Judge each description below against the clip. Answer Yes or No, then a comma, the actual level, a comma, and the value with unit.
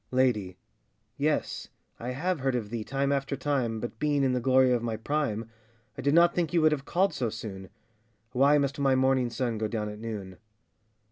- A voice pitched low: Yes, low, 130 Hz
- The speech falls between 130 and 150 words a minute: No, average, 200 wpm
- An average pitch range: Yes, average, 3.9 semitones